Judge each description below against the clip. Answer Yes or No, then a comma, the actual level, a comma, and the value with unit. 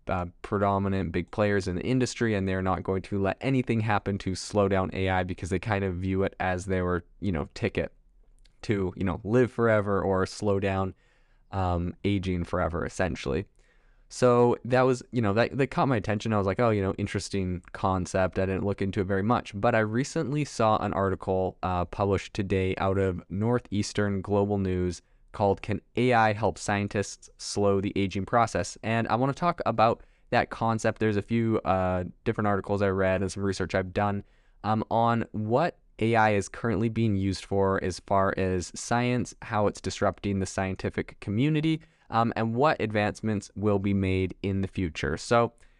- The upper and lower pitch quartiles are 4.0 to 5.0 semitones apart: No, average, 3.2 semitones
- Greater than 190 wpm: No, average, 185 wpm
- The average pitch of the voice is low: Yes, low, 100 Hz